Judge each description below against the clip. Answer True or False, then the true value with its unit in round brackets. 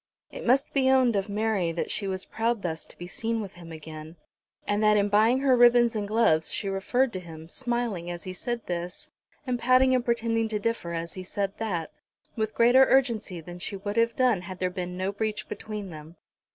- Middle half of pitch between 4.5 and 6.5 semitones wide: True (4.8 semitones)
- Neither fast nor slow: False (215 wpm)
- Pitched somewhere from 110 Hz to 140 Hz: False (210 Hz)